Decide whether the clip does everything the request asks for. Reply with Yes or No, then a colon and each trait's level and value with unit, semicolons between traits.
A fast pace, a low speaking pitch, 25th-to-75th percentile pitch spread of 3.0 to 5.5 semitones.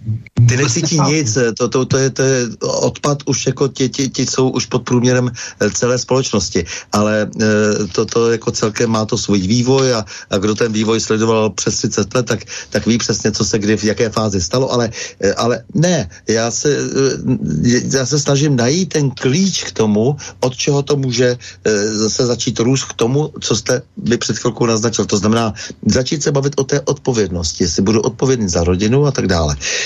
Yes: fast, 190 wpm; low, 120 Hz; average, 3.5 semitones